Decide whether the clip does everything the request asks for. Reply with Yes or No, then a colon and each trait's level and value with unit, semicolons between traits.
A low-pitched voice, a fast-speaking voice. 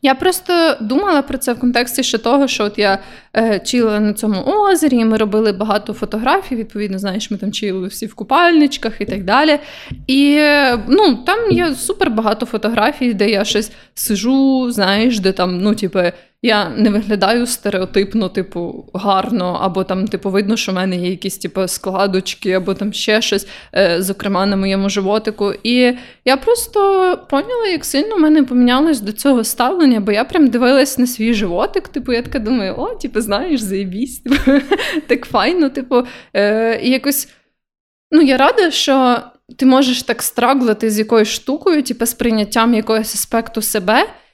No: high, 230 Hz; fast, 170 wpm